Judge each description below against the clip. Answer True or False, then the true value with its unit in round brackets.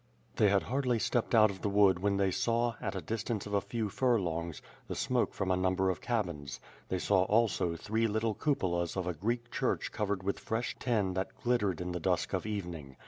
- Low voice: True (100 Hz)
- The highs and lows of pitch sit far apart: False (3.7 semitones)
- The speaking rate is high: True (210 wpm)